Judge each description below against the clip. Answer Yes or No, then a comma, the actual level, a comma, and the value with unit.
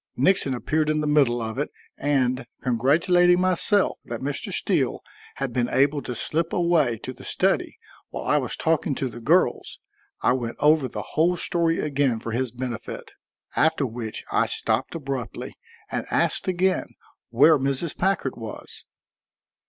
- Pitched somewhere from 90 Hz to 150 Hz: Yes, medium, 140 Hz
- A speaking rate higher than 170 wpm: No, average, 155 wpm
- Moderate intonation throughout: Yes, average, 4.9 semitones